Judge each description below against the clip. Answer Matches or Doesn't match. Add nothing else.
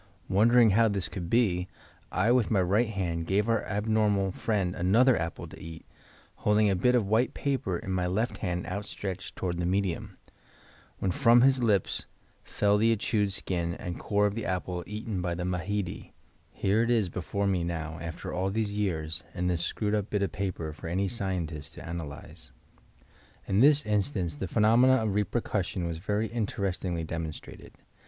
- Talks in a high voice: Doesn't match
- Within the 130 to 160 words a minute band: Doesn't match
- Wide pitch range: Doesn't match